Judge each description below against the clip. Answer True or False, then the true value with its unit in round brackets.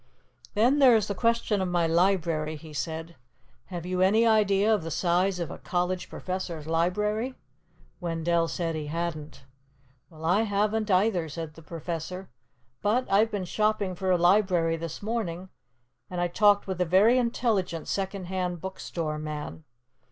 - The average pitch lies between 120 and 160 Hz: False (180 Hz)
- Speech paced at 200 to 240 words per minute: False (160 wpm)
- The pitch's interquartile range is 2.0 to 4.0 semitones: True (3.7 semitones)